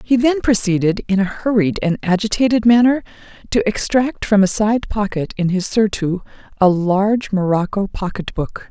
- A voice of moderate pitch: No, high, 205 Hz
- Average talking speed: Yes, average, 160 wpm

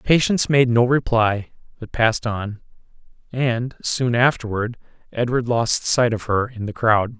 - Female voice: No, male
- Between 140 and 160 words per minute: Yes, average, 150 wpm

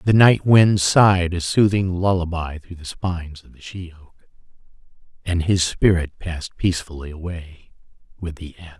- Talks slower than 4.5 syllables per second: No, 5.1 syllables/s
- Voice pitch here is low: Yes, very low, 85 Hz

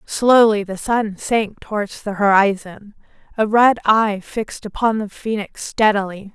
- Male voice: No, female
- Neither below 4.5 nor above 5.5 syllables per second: No, 4.2 syllables/s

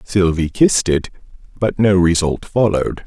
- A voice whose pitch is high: No, very low, 95 Hz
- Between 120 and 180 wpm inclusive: Yes, slow, 135 wpm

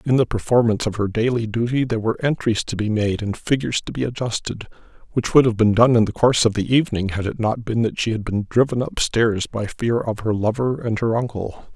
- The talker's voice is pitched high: No, low, 115 Hz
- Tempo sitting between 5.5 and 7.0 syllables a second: Yes, 6.0 syllables/s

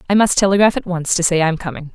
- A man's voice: No, female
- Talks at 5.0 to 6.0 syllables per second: No, 6.8 syllables/s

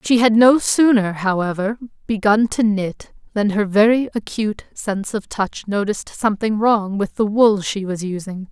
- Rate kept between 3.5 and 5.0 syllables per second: Yes, 4.7 syllables/s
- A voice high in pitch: Yes, high, 210 Hz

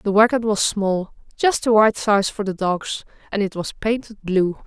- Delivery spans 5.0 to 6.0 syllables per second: No, 4.4 syllables/s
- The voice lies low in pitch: No, high, 210 Hz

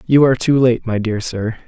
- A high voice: No, low, 120 Hz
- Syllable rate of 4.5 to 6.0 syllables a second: Yes, 5.4 syllables/s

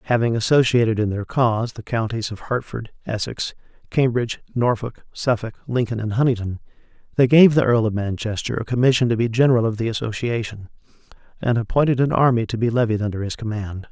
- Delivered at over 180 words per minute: No, average, 170 wpm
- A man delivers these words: Yes, male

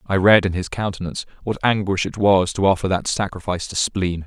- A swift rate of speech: Yes, fast, 210 wpm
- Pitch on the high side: No, very low, 95 Hz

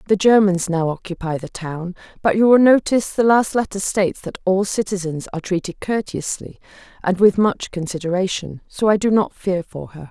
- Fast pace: No, average, 185 wpm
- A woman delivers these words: Yes, female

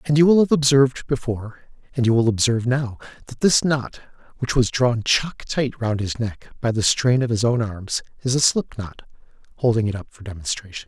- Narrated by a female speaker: No, male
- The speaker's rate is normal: No, fast, 210 wpm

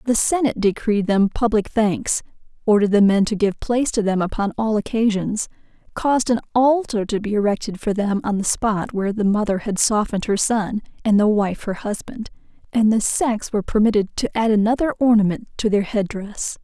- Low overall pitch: No, high, 215 Hz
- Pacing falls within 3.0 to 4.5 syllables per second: No, 5.5 syllables/s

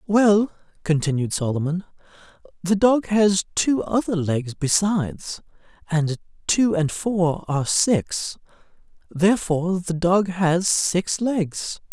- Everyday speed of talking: No, slow, 110 wpm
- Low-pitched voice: No, medium, 180 Hz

